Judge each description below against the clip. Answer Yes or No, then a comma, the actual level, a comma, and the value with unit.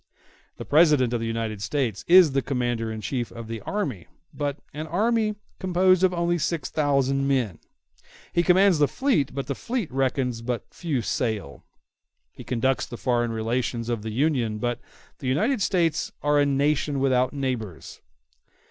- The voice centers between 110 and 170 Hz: Yes, low, 135 Hz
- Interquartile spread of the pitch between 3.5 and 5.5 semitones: Yes, average, 5.2 semitones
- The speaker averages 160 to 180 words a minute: Yes, average, 165 wpm